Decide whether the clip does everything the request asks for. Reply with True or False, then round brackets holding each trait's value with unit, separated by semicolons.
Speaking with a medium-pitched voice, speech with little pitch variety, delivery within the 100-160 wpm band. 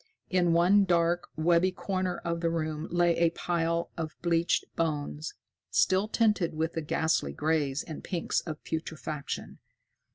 True (170 Hz; 1.8 semitones; 140 wpm)